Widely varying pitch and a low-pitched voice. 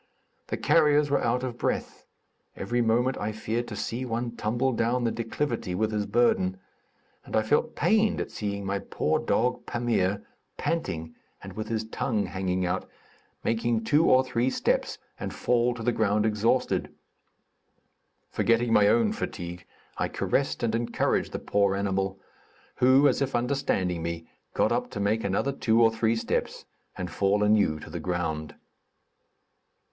No: average, 3.7 semitones; low, 110 Hz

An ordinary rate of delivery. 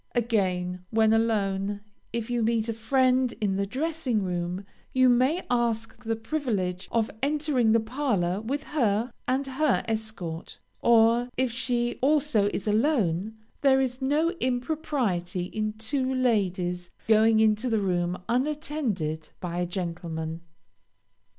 No: slow, 130 wpm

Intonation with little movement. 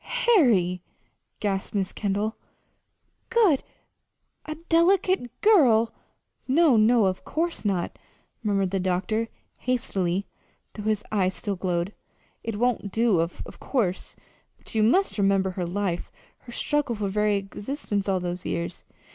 No: average, 4.6 semitones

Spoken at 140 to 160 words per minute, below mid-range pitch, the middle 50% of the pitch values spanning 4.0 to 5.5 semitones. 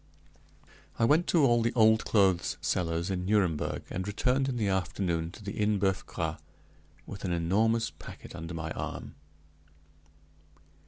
Yes: average, 150 wpm; low, 100 Hz; average, 4.3 semitones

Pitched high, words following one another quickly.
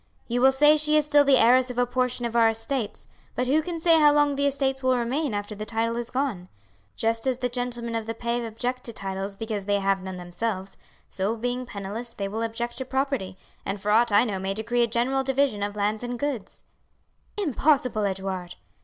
Yes: high, 235 Hz; fast, 215 wpm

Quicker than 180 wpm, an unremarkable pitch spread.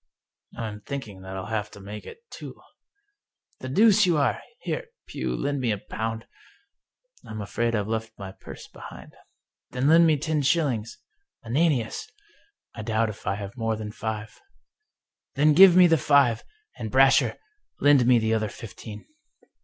No: average, 190 wpm; wide, 5.9 semitones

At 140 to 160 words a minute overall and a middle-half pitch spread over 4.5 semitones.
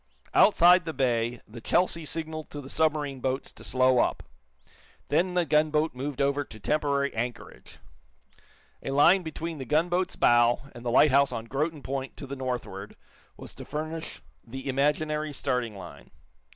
No: average, 155 wpm; average, 3.7 semitones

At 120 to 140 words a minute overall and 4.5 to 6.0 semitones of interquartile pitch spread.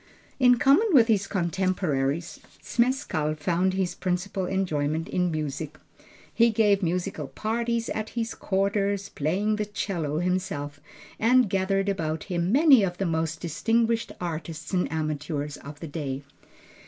Yes: slow, 135 wpm; average, 5.0 semitones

